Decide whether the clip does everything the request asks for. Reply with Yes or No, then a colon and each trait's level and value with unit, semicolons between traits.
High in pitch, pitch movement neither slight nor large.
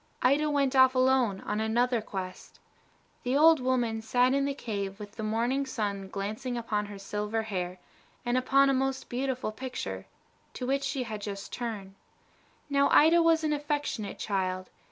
Yes: high, 245 Hz; average, 4.5 semitones